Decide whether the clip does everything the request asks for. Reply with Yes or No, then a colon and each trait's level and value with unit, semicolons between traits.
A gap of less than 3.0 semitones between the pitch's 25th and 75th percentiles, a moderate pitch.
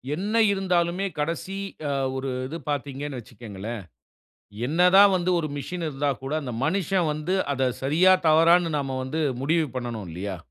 No: average, 4.7 semitones; medium, 150 Hz